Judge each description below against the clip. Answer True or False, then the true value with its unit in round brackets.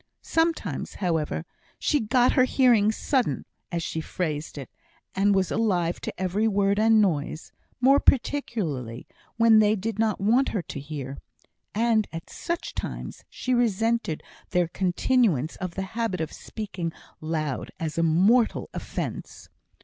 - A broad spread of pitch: True (5.7 semitones)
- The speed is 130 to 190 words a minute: True (140 wpm)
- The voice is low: False (200 Hz)